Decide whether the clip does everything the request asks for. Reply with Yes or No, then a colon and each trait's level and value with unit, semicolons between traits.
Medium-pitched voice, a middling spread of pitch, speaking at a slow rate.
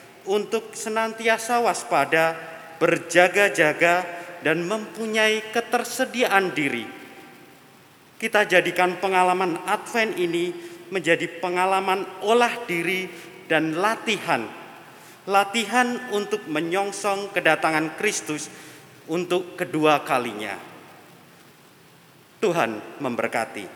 Yes: medium, 180 Hz; average, 4.1 semitones; slow, 75 wpm